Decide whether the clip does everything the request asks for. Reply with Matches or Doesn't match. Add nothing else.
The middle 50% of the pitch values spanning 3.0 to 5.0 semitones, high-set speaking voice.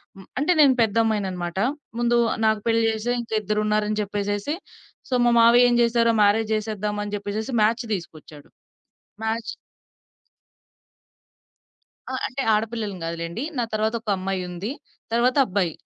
Doesn't match